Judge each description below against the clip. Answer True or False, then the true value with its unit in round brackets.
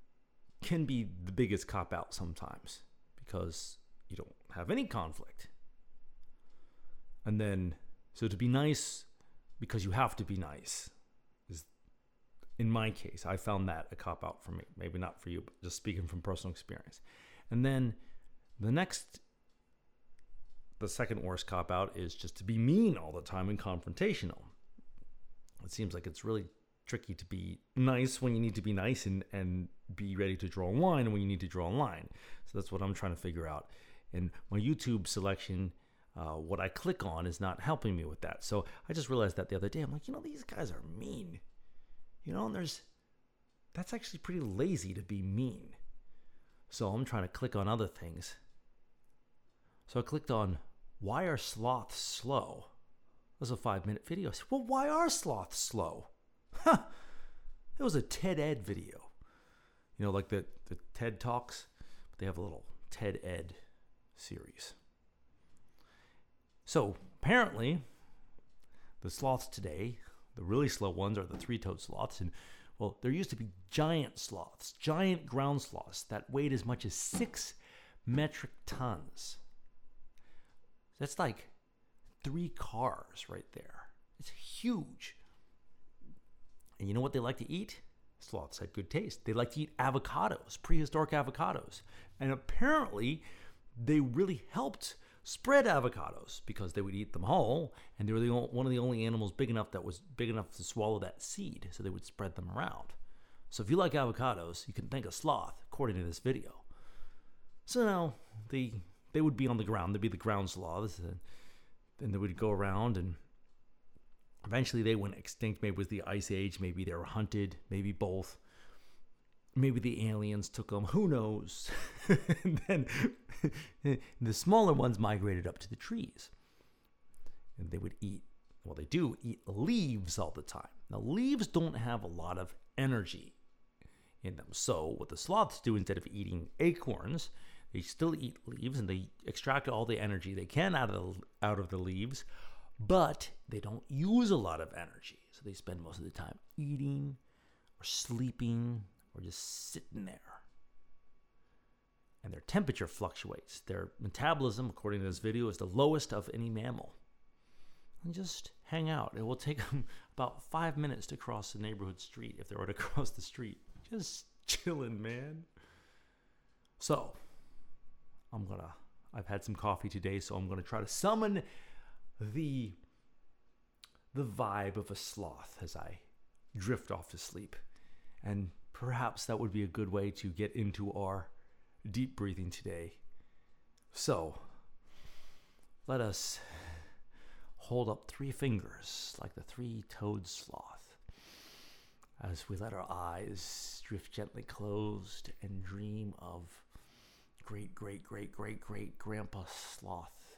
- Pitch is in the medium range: False (105 Hz)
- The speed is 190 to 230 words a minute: False (165 wpm)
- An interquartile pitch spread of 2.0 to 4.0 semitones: False (5.3 semitones)